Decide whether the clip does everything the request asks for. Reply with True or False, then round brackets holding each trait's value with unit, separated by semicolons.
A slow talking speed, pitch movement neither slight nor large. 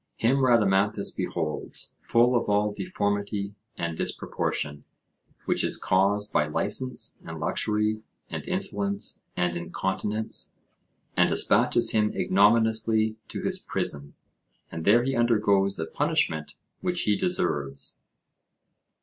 True (115 wpm; 3.2 semitones)